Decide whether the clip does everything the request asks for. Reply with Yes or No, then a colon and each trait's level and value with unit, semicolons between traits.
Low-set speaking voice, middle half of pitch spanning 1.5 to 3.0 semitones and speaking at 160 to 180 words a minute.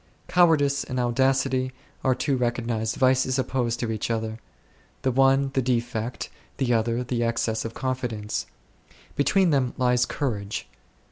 No: low, 125 Hz; narrow, 2.4 semitones; slow, 135 wpm